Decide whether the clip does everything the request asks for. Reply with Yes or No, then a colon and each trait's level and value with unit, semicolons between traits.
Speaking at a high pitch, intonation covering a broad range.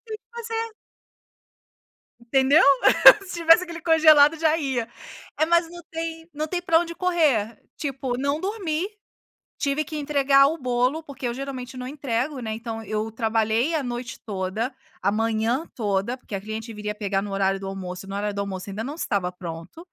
Yes: very high, 255 Hz; wide, 6.5 semitones